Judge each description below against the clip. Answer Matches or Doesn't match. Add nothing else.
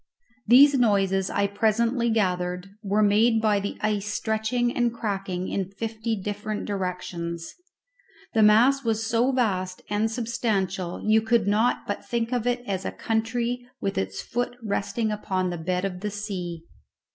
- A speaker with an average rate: Matches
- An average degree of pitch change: Matches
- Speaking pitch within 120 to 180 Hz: Doesn't match